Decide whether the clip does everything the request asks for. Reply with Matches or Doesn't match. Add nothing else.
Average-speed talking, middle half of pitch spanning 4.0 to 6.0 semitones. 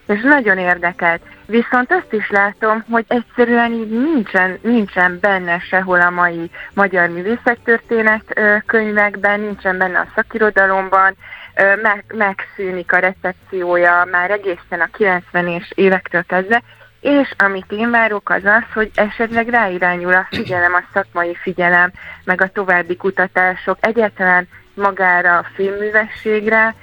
Doesn't match